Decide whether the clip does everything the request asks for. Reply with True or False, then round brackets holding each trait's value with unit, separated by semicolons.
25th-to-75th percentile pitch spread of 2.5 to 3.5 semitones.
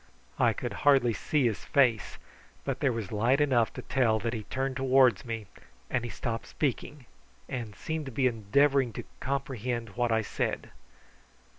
True (3.0 semitones)